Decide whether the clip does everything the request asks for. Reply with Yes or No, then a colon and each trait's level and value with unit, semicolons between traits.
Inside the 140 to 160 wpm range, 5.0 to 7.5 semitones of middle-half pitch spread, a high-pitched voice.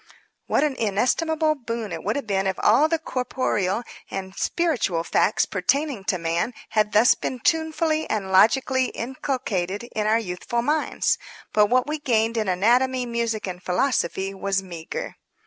Yes: average, 155 wpm; average, 5.3 semitones; high, 225 Hz